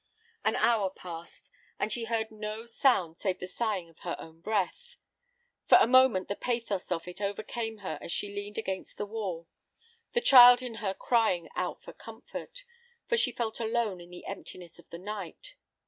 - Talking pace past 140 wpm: Yes, average, 180 wpm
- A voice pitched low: No, high, 210 Hz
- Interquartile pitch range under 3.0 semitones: No, average, 4.4 semitones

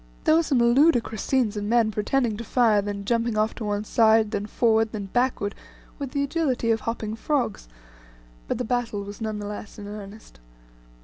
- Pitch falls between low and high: No, high, 225 Hz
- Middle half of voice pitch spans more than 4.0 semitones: No, average, 2.8 semitones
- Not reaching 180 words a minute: No, average, 190 wpm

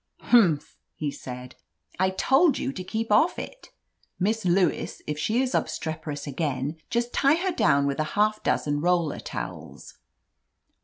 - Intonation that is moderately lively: No, wide, 7.7 semitones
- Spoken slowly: No, average, 155 wpm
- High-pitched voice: No, medium, 180 Hz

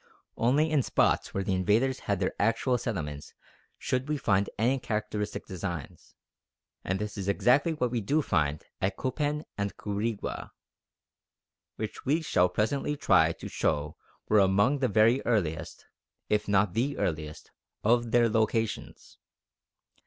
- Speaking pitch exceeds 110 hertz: No, low, 105 Hz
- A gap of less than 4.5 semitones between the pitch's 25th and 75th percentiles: No, average, 4.8 semitones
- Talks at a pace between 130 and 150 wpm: Yes, average, 140 wpm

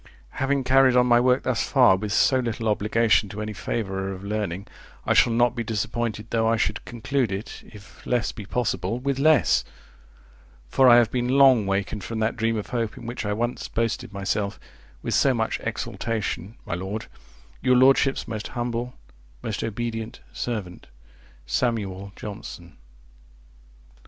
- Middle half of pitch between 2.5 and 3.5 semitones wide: Yes, average, 2.9 semitones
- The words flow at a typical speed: Yes, average, 160 wpm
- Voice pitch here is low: Yes, low, 115 Hz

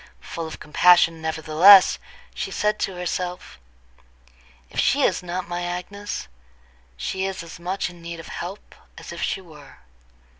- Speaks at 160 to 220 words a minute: No, average, 150 wpm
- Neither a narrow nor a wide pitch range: No, narrow, 2.2 semitones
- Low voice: No, medium, 175 Hz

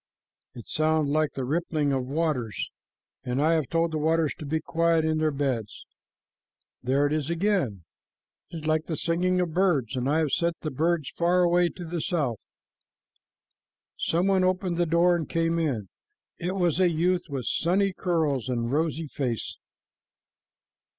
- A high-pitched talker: No, medium, 160 Hz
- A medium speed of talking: Yes, average, 170 wpm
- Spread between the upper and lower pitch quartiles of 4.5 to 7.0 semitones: No, average, 3.4 semitones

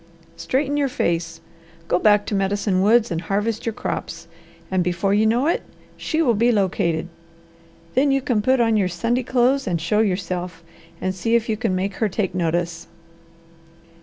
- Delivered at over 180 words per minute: No, average, 175 wpm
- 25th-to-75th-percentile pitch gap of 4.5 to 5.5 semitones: Yes, average, 4.8 semitones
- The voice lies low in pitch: No, high, 205 Hz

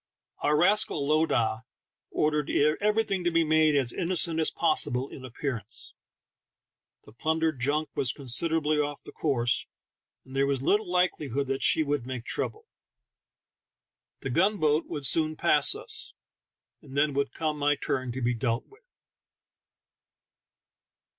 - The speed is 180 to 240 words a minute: No, average, 140 wpm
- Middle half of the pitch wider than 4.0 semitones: No, average, 3.5 semitones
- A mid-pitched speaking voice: Yes, medium, 150 Hz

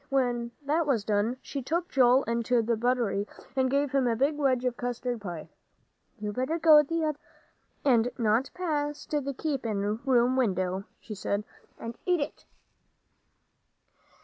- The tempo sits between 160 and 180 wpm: No, average, 150 wpm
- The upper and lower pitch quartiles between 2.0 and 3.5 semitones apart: No, average, 4.0 semitones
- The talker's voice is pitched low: No, very high, 250 Hz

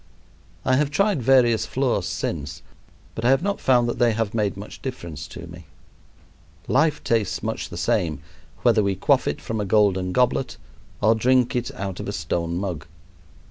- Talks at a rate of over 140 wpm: Yes, average, 180 wpm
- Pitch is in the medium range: No, low, 115 Hz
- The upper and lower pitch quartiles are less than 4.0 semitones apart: No, average, 4.7 semitones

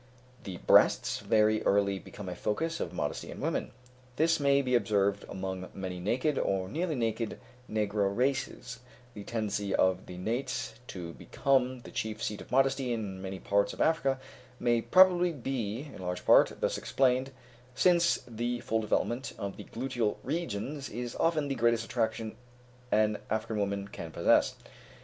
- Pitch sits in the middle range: No, low, 115 Hz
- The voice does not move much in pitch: No, average, 4.9 semitones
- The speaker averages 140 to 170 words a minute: Yes, average, 160 wpm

